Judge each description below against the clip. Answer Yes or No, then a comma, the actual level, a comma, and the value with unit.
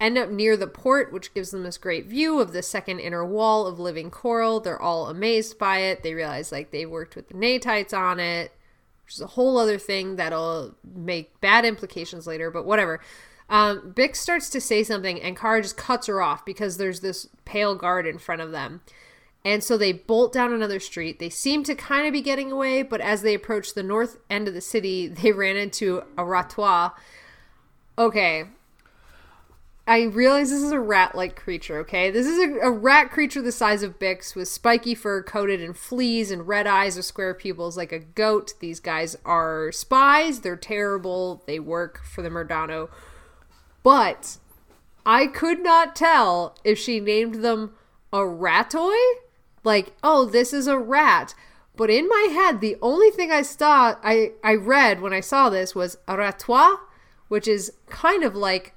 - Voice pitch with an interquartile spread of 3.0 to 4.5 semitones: No, average, 5.1 semitones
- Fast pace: No, average, 190 wpm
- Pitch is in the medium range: No, high, 205 Hz